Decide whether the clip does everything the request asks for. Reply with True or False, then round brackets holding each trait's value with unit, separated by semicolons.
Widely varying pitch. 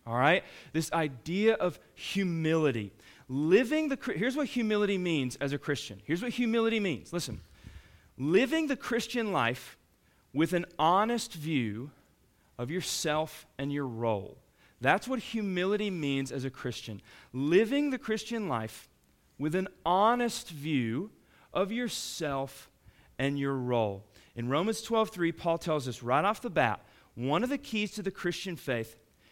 True (8.9 semitones)